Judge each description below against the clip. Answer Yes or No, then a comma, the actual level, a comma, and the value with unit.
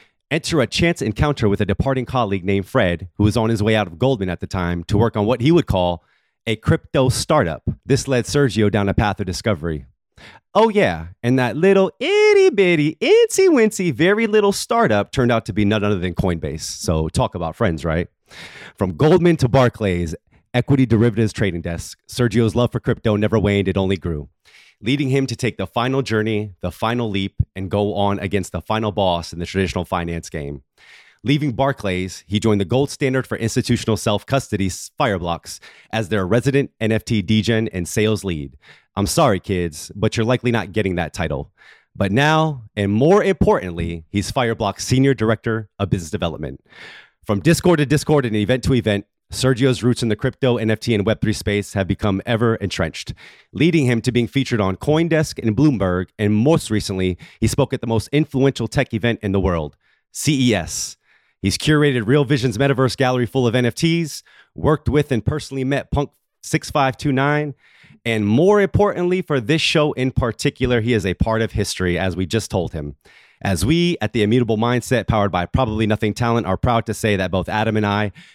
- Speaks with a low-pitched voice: Yes, low, 110 Hz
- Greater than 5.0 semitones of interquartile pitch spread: Yes, wide, 5.5 semitones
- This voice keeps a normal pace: Yes, average, 185 wpm